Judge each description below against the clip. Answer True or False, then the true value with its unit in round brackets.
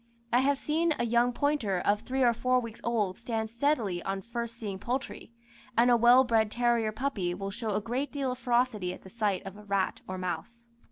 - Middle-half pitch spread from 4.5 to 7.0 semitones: False (3.5 semitones)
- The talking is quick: True (215 wpm)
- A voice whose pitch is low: False (235 Hz)